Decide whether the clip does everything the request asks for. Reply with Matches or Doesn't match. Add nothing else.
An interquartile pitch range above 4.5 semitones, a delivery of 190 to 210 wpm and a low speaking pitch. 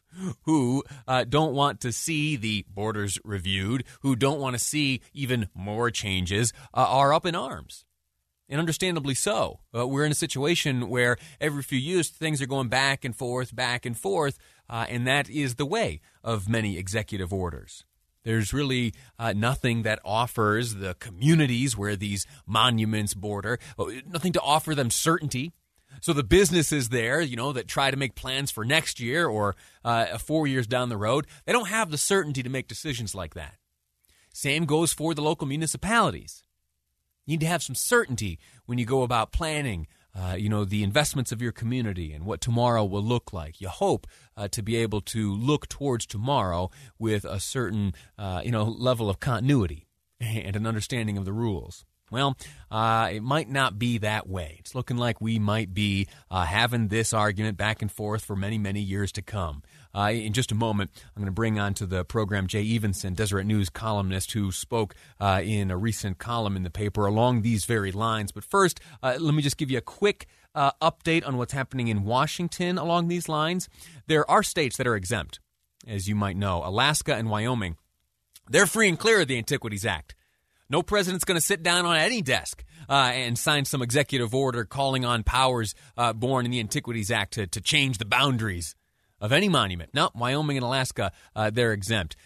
Matches